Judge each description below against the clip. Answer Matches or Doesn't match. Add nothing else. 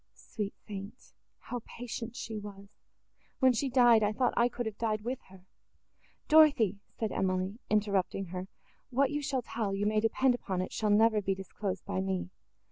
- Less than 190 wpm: Matches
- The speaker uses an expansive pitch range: Doesn't match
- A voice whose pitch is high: Matches